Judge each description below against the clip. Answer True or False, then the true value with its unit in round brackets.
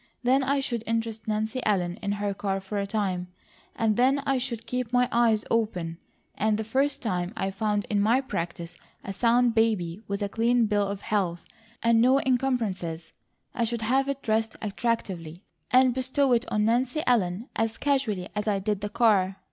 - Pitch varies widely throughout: False (3.7 semitones)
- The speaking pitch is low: False (220 Hz)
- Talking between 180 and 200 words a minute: True (185 wpm)